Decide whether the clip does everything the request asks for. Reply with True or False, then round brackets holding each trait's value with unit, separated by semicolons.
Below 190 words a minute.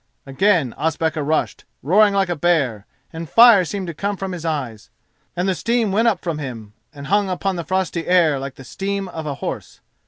False (200 wpm)